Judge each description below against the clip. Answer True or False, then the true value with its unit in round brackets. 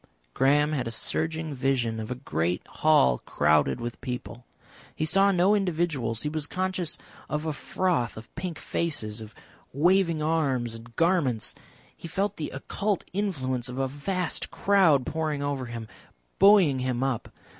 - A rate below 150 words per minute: False (155 wpm)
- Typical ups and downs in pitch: False (5.7 semitones)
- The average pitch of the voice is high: False (145 Hz)